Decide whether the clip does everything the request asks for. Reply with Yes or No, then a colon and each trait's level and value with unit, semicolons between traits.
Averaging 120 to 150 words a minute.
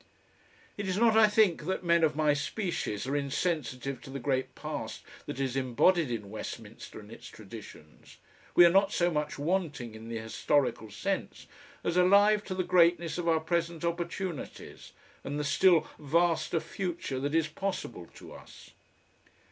No: average, 165 wpm